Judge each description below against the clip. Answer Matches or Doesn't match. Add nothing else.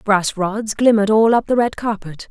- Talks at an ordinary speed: Doesn't match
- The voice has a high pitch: Matches